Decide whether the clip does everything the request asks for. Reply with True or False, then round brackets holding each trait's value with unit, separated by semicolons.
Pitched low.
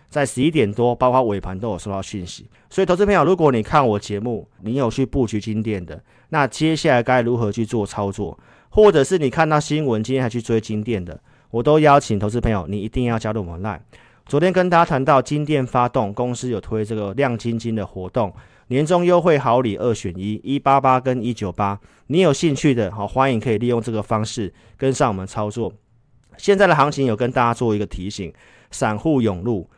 True (120 Hz)